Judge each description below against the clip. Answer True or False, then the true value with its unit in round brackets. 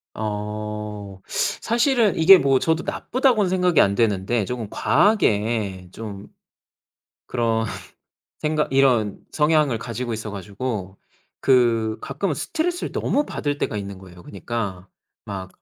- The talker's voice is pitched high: False (115 Hz)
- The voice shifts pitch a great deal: True (6.8 semitones)